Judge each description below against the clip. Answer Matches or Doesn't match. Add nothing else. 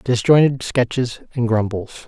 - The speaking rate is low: Matches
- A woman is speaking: Doesn't match